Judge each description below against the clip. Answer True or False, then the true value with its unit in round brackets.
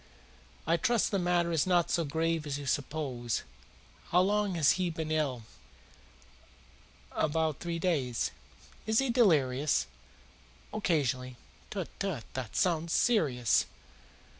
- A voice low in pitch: False (160 Hz)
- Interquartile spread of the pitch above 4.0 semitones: True (4.5 semitones)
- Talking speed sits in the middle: False (120 wpm)